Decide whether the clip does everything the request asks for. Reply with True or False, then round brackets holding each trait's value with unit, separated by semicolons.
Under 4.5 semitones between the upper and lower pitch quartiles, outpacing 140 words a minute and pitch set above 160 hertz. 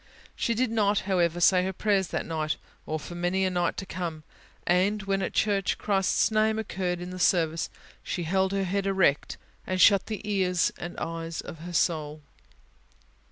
True (2.5 semitones; 180 wpm; 185 Hz)